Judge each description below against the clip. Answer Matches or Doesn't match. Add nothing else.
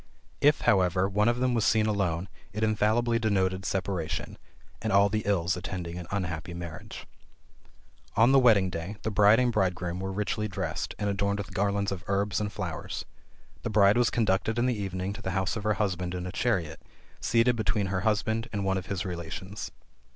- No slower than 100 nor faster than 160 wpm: Doesn't match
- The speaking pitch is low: Matches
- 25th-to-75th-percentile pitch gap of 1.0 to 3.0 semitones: Matches